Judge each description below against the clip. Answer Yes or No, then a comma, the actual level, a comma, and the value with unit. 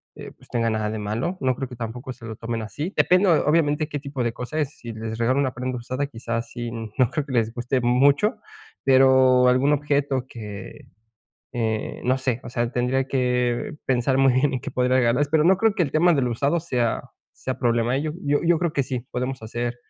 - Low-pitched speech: Yes, low, 130 Hz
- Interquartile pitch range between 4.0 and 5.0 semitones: No, average, 3.1 semitones